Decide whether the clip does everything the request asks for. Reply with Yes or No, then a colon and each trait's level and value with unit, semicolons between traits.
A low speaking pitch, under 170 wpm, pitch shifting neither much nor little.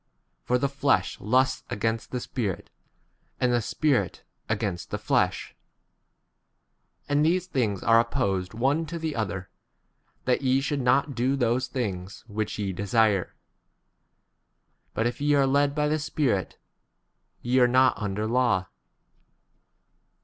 Yes: low, 125 Hz; average, 140 wpm; average, 4.8 semitones